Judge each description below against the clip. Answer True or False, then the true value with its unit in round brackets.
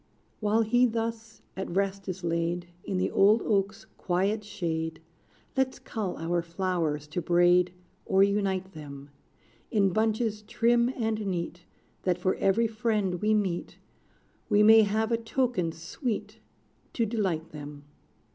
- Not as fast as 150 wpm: True (135 wpm)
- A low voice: False (195 Hz)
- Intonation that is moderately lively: True (4.0 semitones)